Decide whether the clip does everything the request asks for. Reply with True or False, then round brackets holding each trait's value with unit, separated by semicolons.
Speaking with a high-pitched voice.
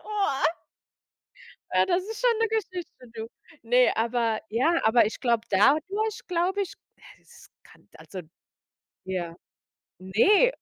True (270 Hz)